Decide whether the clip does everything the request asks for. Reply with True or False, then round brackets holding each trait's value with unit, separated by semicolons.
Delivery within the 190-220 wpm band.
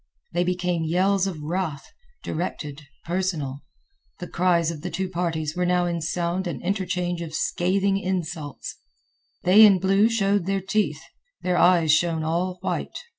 False (150 wpm)